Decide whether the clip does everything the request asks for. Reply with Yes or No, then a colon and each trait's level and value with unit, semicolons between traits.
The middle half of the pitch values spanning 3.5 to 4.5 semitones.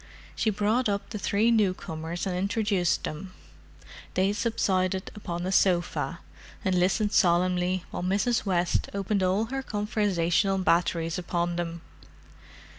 No: average, 2.8 semitones